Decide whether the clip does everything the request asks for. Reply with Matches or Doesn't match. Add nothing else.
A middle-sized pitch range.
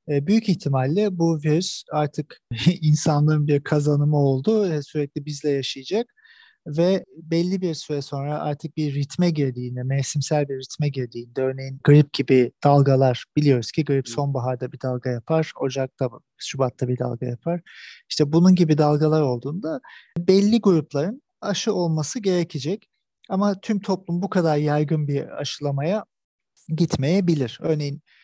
Matches